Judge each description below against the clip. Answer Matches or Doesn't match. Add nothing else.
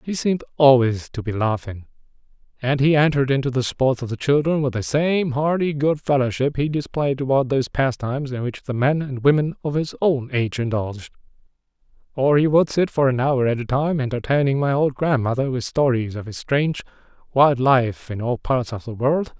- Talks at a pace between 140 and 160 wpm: Doesn't match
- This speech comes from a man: Matches